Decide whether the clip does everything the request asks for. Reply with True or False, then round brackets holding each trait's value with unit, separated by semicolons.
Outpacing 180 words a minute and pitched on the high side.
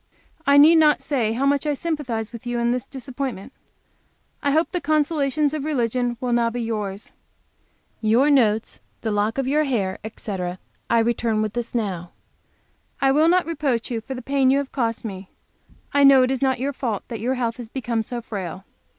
True (195 wpm; 245 Hz)